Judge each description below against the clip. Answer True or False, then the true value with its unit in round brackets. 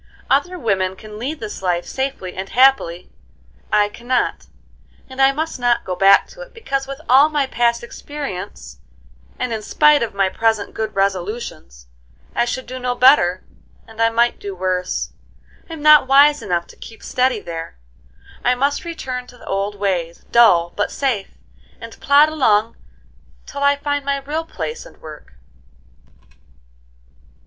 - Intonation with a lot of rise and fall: True (5.9 semitones)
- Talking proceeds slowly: False (160 wpm)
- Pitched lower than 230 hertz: False (235 Hz)